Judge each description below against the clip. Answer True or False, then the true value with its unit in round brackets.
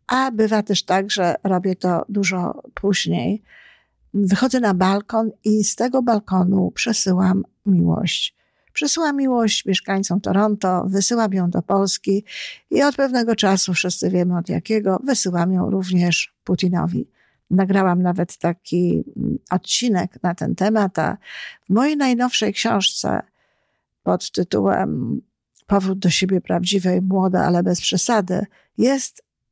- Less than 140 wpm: True (120 wpm)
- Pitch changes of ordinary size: True (3.2 semitones)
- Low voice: False (195 Hz)